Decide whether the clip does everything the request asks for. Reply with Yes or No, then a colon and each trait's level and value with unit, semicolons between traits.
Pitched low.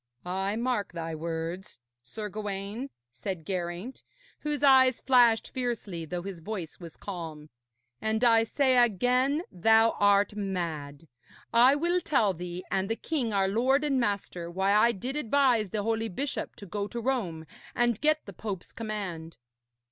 No: high, 210 Hz